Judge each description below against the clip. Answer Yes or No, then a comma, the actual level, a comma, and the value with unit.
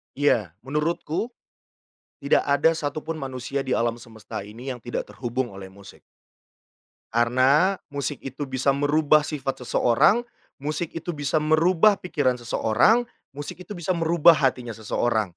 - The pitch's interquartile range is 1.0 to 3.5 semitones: No, average, 4.6 semitones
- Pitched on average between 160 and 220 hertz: No, medium, 140 Hz